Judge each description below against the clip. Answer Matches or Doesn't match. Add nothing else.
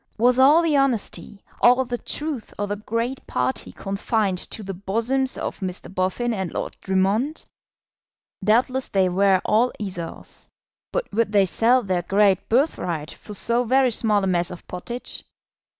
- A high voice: Matches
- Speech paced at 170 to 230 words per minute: Doesn't match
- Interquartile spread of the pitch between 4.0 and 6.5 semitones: Matches